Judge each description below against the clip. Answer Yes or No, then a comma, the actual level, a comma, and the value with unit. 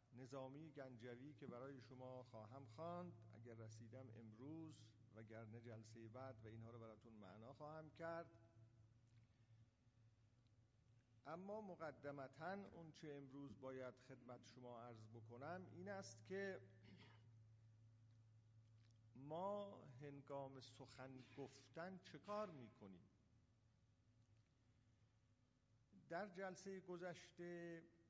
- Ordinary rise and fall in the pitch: Yes, average, 4.8 semitones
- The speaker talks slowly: Yes, slow, 90 wpm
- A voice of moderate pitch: No, low, 120 Hz